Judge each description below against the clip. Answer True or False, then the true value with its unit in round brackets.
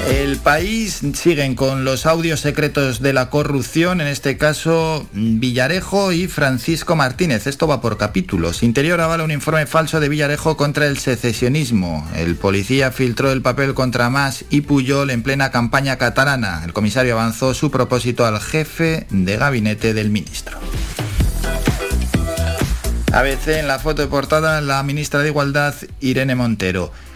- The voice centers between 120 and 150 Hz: True (135 Hz)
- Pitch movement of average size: True (4.2 semitones)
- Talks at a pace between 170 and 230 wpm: False (150 wpm)